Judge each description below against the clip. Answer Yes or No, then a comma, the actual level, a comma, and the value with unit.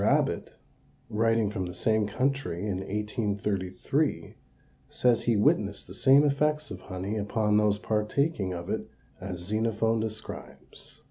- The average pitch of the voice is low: Yes, low, 105 Hz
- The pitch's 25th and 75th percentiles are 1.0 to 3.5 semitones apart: Yes, narrow, 2.6 semitones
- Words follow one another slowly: Yes, slow, 130 wpm